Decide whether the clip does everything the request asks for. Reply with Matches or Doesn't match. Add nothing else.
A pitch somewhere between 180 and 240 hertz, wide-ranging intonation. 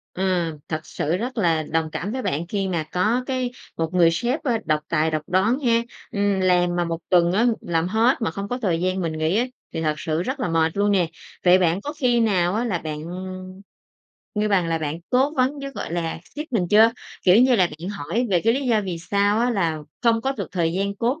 Matches